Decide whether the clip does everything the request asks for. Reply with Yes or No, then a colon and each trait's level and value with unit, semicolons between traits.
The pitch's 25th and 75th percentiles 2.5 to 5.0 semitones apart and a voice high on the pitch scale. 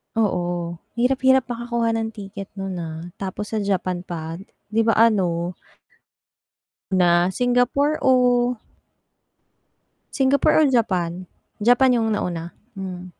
No: wide, 5.5 semitones; high, 205 Hz